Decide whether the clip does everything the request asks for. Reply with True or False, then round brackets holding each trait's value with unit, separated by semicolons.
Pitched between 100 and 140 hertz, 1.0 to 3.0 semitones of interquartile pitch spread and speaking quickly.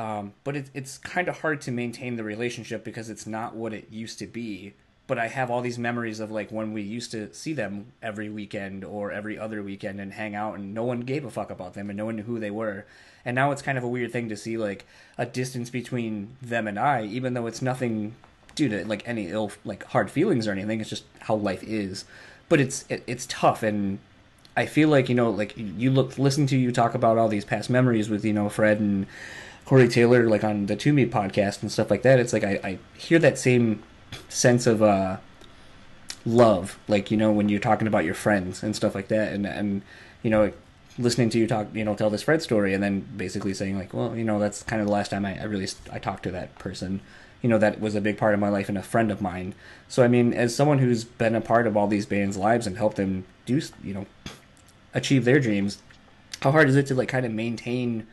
True (110 Hz; 2.7 semitones; 250 wpm)